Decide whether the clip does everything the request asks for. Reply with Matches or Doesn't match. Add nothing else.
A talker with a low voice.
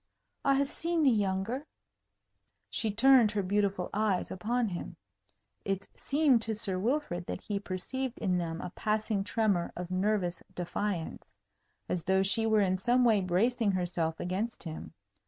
Doesn't match